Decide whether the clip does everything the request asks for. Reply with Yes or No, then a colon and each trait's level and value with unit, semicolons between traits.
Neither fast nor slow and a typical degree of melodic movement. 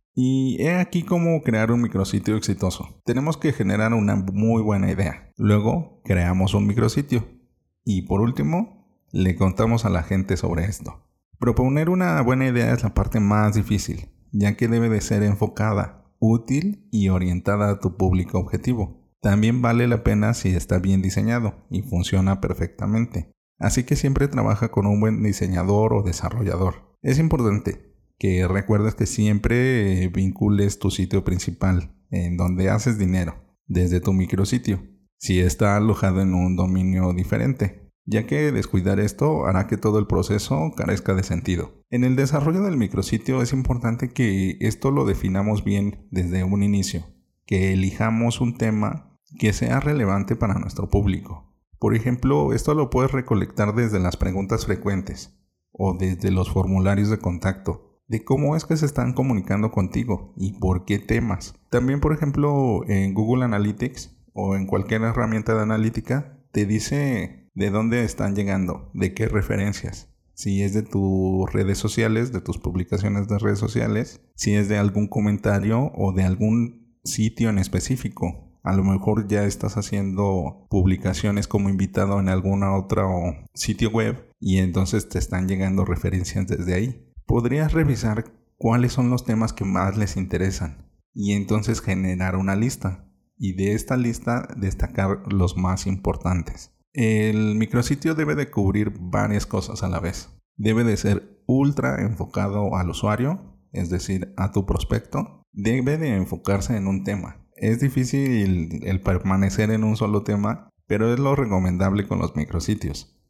Yes: average, 155 wpm; average, 3.5 semitones